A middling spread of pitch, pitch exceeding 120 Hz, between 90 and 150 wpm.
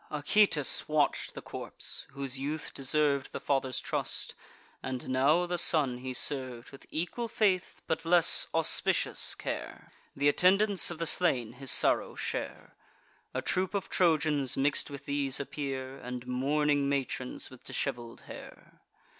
Yes: average, 3.6 semitones; medium, 140 Hz; average, 140 wpm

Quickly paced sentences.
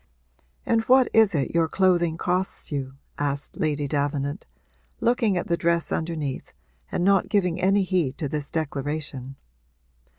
No: average, 140 wpm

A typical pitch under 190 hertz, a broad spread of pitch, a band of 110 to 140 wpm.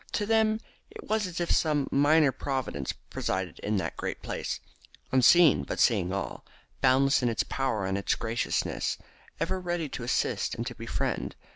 No: low, 135 Hz; wide, 7.3 semitones; average, 165 wpm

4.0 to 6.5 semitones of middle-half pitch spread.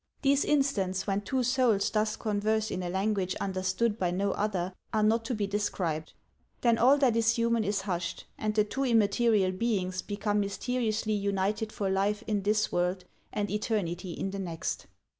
No: average, 2.9 semitones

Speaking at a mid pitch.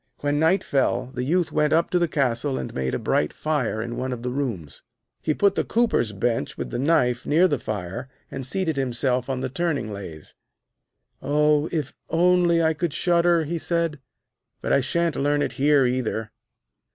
Yes: medium, 145 Hz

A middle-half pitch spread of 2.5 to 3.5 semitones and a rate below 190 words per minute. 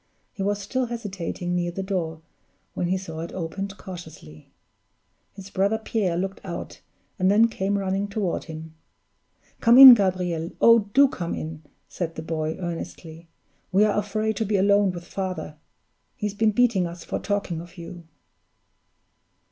Yes: average, 3.2 semitones; average, 155 wpm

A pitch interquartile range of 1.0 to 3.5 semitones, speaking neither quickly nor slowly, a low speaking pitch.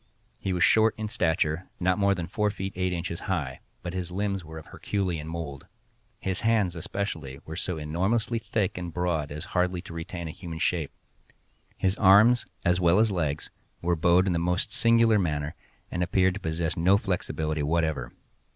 Yes: average, 3.2 semitones; average, 180 wpm; very low, 90 Hz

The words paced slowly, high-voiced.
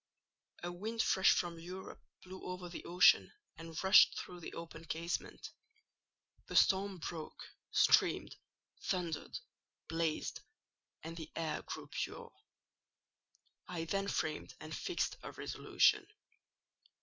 No: slow, 115 wpm; medium, 175 Hz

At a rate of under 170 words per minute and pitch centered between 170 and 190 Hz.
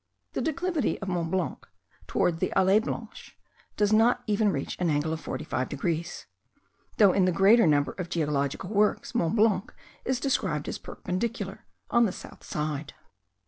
Yes: average, 160 wpm; medium, 185 Hz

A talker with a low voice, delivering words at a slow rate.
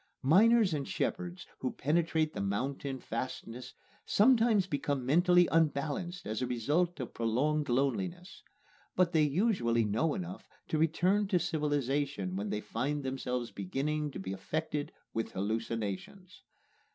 No: medium, 145 Hz; slow, 130 wpm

